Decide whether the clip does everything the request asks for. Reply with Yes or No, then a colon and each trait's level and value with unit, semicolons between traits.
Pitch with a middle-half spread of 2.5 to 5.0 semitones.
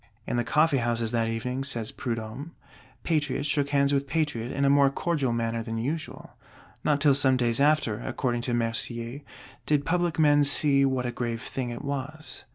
Yes: average, 3.6 semitones